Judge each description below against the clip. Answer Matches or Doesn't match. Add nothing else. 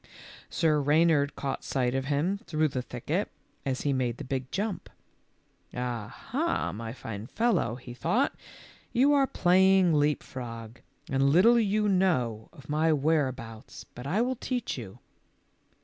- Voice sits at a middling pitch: Matches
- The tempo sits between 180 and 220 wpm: Doesn't match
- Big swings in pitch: Matches